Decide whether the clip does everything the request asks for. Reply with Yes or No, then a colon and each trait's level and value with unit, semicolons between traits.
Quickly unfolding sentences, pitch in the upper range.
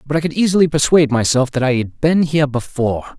No: fast, 225 wpm; medium, 145 Hz